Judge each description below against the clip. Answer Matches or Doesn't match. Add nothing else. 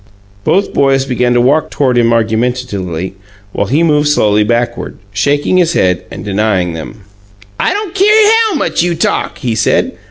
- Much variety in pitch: Matches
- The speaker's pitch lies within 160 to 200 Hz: Doesn't match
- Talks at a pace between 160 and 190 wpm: Matches